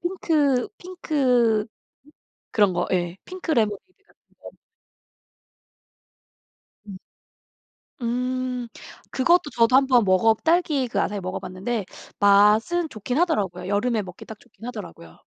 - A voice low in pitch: No, high, 235 Hz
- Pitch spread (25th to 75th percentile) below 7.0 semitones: Yes, wide, 5.6 semitones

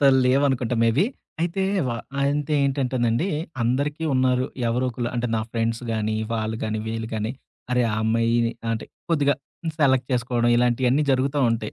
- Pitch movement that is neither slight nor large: Yes, average, 3.2 semitones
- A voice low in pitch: Yes, low, 125 Hz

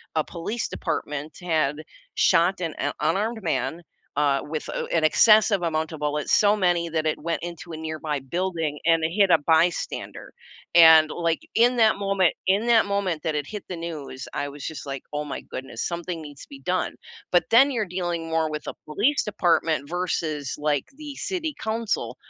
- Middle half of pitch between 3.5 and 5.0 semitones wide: Yes, average, 4.0 semitones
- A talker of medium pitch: Yes, medium, 165 Hz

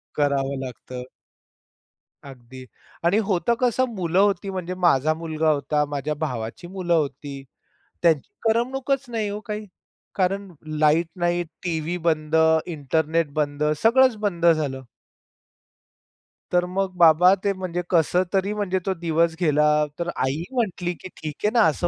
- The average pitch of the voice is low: No, medium, 170 Hz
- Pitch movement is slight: No, average, 4.3 semitones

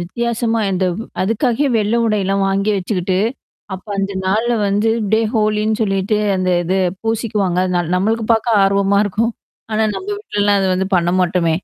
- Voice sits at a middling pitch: No, high, 205 Hz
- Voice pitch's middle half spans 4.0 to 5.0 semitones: No, average, 2.9 semitones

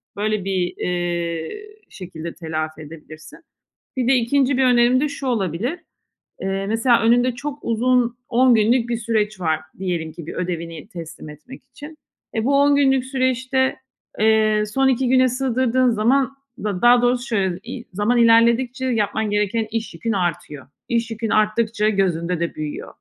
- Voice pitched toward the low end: No, high, 225 Hz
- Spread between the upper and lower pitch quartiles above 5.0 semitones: Yes, wide, 5.6 semitones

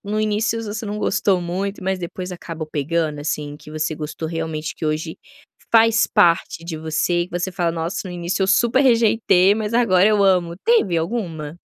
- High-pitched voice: No, medium, 180 Hz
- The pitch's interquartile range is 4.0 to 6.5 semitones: Yes, average, 4.5 semitones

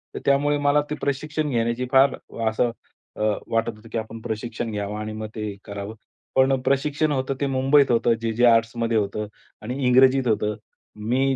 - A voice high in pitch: No, low, 120 Hz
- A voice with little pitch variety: No, average, 3.6 semitones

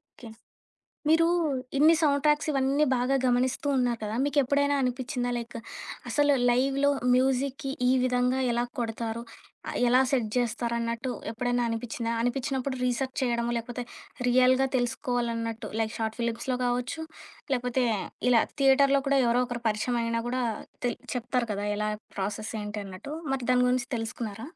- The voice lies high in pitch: Yes, high, 245 Hz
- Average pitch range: No, narrow, 2.3 semitones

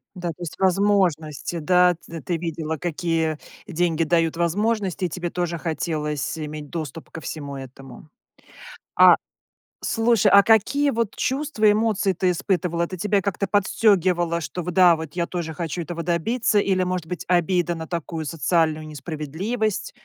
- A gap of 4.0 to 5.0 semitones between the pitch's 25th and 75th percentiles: No, average, 3.3 semitones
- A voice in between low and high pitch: Yes, medium, 175 Hz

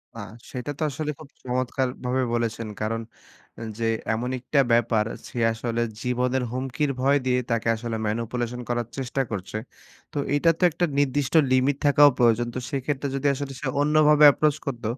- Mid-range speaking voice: No, low, 125 Hz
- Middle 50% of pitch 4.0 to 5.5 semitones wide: No, average, 3.3 semitones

